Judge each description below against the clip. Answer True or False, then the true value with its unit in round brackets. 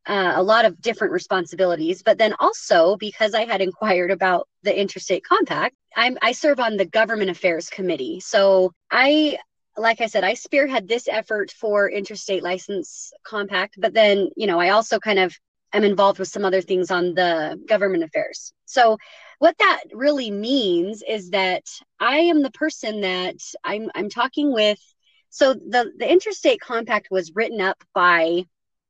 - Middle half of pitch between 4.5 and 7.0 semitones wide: True (5.4 semitones)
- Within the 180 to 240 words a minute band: False (170 wpm)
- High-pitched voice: True (210 Hz)